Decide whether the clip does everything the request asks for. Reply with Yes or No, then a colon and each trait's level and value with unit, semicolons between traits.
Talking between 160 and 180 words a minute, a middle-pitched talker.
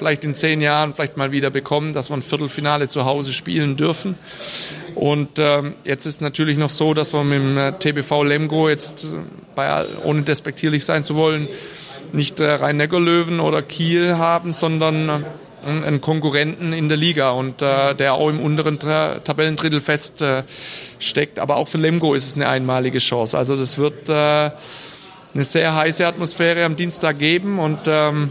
Yes: average, 170 wpm; medium, 150 Hz